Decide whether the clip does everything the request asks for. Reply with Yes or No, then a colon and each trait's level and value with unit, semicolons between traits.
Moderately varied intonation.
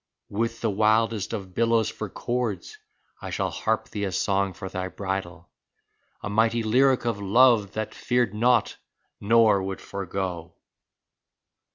Yes: average, 3.0 semitones